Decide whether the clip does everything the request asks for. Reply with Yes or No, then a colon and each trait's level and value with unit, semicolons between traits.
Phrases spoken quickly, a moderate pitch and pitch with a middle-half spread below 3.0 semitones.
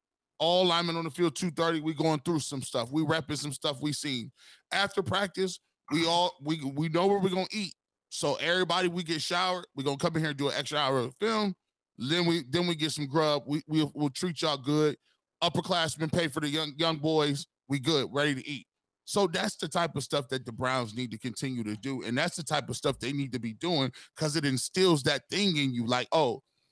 No: fast, 245 wpm; medium, 155 Hz; average, 3.5 semitones